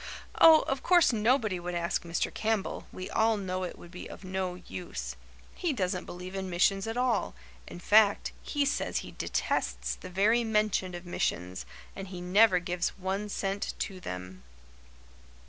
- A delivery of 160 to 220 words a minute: Yes, average, 165 wpm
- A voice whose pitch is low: No, high, 190 Hz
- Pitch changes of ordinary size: Yes, average, 3.5 semitones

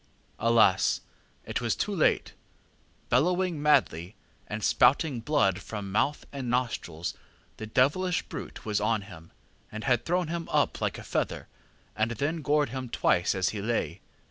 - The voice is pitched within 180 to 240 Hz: No, low, 115 Hz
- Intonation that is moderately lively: No, wide, 6.4 semitones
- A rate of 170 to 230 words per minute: No, average, 150 wpm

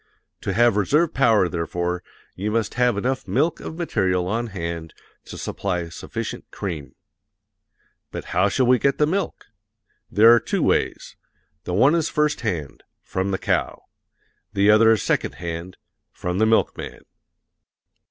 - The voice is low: Yes, low, 105 Hz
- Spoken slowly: No, average, 150 wpm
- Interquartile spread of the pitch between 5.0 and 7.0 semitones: Yes, wide, 5.4 semitones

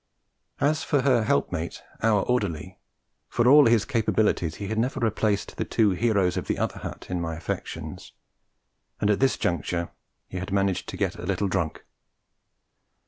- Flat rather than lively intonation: No, average, 4.8 semitones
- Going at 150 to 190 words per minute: Yes, average, 165 wpm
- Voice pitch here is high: No, low, 100 Hz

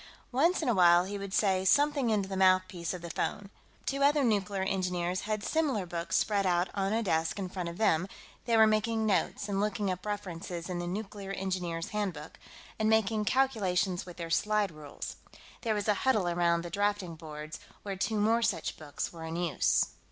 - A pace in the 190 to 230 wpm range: Yes, average, 195 wpm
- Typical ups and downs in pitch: Yes, average, 3.5 semitones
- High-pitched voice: Yes, high, 195 Hz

